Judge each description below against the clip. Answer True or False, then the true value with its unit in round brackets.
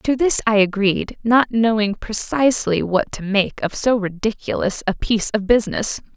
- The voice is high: True (215 Hz)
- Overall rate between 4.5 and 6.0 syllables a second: True (4.8 syllables/s)